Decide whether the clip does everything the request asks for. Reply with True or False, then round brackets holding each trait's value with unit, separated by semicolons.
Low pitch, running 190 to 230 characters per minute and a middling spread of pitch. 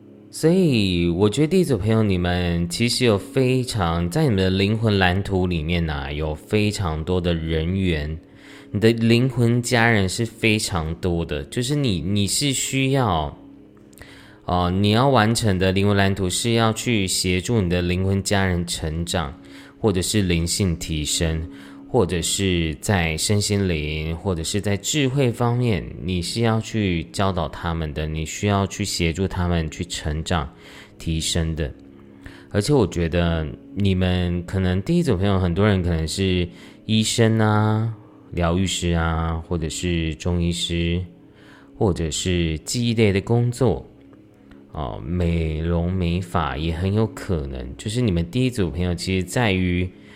True (95 Hz; 225 characters per minute; 4.3 semitones)